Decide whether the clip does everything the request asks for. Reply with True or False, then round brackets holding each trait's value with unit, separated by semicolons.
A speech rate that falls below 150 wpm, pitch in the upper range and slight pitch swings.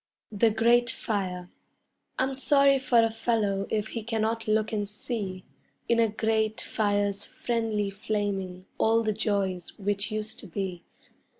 True (140 wpm; 215 Hz; 2.3 semitones)